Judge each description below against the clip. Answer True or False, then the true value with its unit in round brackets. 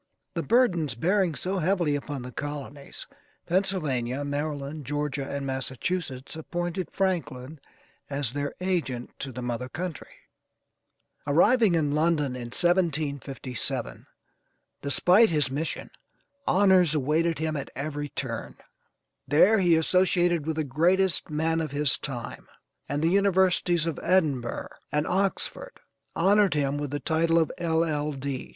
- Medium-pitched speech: True (155 Hz)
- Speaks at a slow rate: True (125 wpm)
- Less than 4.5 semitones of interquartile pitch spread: True (3.9 semitones)